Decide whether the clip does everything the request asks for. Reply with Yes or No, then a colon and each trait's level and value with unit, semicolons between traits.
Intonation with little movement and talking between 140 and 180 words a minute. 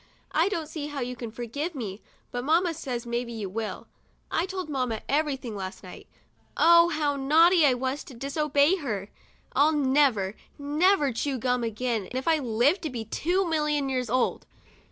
No: average, 4.5 semitones; average, 175 wpm